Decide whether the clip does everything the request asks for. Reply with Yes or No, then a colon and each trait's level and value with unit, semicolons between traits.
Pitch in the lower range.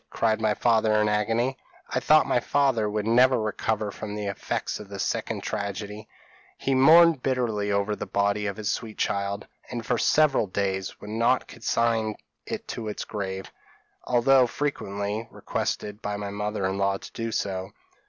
Yes: low, 105 Hz